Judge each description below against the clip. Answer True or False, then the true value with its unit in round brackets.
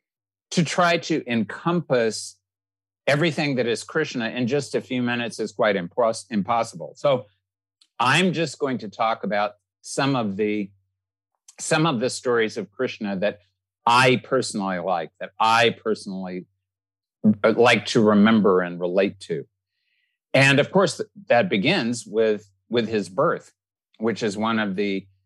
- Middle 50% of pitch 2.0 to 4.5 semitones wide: False (5.6 semitones)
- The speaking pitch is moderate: False (110 Hz)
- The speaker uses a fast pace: False (145 wpm)